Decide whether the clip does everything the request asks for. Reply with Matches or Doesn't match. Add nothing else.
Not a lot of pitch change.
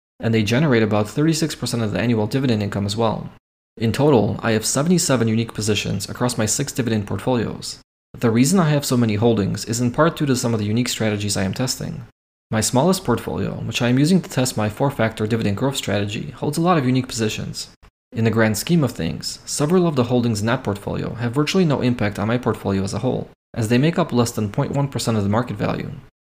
Doesn't match